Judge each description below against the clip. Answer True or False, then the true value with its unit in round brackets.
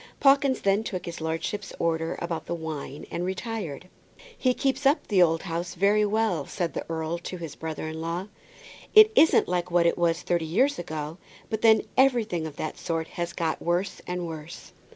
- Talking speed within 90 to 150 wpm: False (190 wpm)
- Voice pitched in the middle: True (175 Hz)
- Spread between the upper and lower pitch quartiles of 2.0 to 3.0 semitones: False (4.3 semitones)